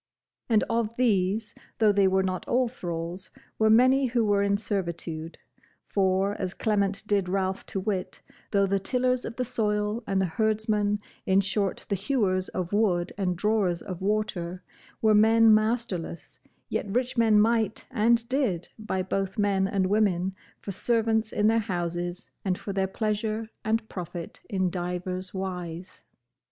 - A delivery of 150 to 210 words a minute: Yes, average, 155 wpm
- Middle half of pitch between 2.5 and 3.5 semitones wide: Yes, average, 2.8 semitones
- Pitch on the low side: No, high, 200 Hz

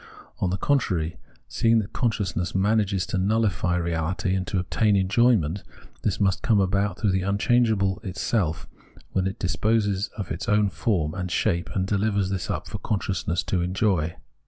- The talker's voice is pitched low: Yes, very low, 95 Hz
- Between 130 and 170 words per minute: Yes, average, 165 wpm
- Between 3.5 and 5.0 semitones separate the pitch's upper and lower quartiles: No, narrow, 2.6 semitones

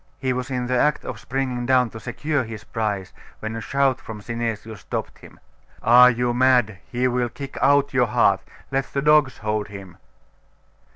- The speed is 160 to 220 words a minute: Yes, average, 180 wpm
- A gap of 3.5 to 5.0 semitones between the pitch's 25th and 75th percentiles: No, average, 3.0 semitones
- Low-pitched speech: Yes, low, 125 Hz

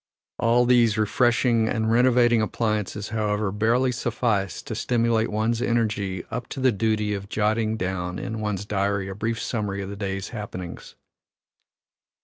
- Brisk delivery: No, average, 145 wpm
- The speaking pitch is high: No, low, 110 Hz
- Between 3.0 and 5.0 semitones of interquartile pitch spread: No, narrow, 2.6 semitones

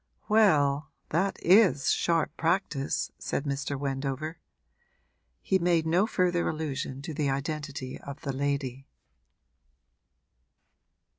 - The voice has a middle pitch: Yes, medium, 150 Hz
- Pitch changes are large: No, average, 3.5 semitones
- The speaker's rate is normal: No, slow, 100 wpm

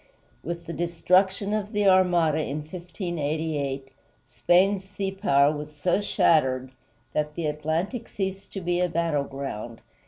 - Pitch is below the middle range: No, medium, 170 Hz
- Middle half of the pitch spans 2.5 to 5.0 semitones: Yes, average, 4.2 semitones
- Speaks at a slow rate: Yes, slow, 130 wpm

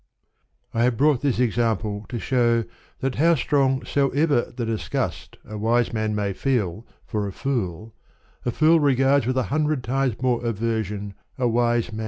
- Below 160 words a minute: No, average, 170 wpm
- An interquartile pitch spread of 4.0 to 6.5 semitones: No, average, 3.6 semitones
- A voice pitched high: No, low, 120 Hz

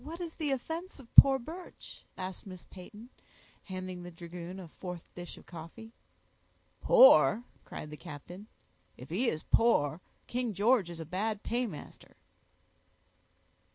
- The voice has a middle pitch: No, high, 195 Hz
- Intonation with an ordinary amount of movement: No, wide, 6.0 semitones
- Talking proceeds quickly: No, average, 140 wpm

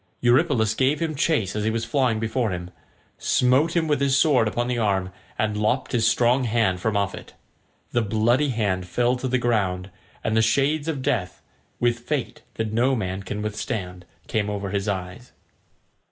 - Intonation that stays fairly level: No, average, 4.0 semitones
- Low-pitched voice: Yes, low, 115 Hz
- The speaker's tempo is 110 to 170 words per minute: No, average, 180 wpm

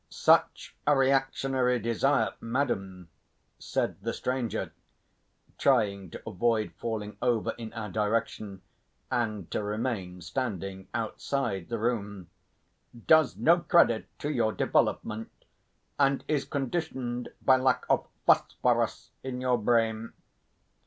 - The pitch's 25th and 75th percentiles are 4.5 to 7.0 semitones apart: No, average, 3.9 semitones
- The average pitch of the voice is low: Yes, low, 115 Hz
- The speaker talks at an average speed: No, slow, 110 wpm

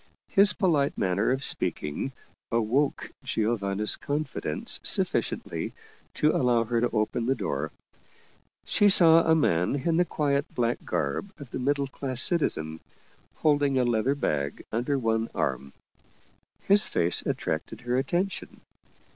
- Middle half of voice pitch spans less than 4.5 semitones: No, average, 5.2 semitones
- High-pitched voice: No, low, 130 Hz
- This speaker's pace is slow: Yes, slow, 130 wpm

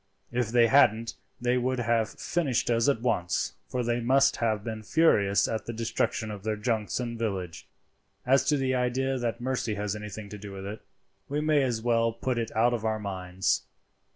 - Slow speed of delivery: No, average, 195 wpm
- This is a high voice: No, low, 115 Hz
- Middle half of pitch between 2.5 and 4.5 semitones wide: Yes, average, 2.8 semitones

